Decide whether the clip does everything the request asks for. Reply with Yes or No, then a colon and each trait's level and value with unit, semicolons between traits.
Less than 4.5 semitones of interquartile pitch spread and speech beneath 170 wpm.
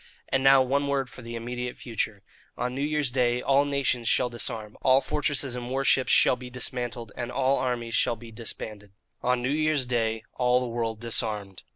No: narrow, 2.4 semitones; average, 200 wpm